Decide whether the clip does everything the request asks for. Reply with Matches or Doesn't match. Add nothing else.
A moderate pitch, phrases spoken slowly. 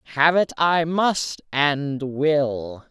Matches